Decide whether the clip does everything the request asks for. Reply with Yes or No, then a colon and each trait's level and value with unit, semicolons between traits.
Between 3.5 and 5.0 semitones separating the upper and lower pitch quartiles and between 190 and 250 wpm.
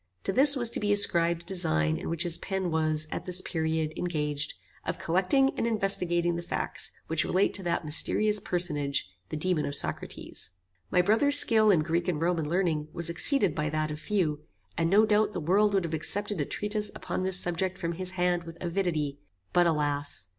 Yes: average, 3.8 semitones; average, 195 wpm